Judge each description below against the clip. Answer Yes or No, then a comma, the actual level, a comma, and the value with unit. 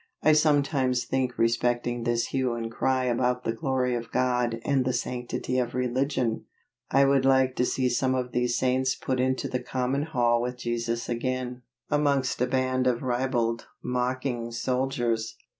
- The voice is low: Yes, low, 125 Hz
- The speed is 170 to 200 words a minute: No, average, 160 wpm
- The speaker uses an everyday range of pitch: No, narrow, 1.4 semitones